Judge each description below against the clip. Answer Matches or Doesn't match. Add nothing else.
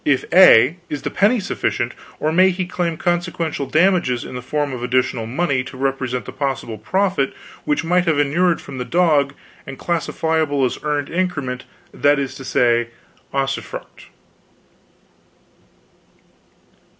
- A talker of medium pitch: Matches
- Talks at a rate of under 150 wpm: Matches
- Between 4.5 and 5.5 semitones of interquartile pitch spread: Matches